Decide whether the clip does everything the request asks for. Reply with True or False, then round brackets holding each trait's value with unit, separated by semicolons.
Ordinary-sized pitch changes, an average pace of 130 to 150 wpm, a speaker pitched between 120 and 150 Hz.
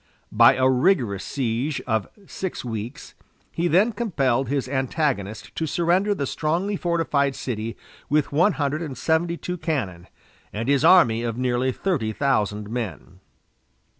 False (6.2 semitones; 140 wpm; 140 Hz)